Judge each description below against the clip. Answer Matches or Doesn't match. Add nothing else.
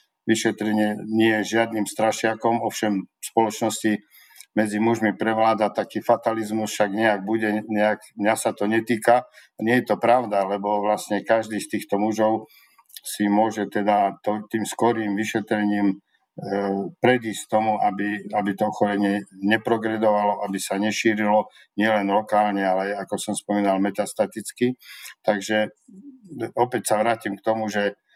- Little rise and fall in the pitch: Matches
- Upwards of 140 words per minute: Doesn't match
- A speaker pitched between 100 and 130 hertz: Matches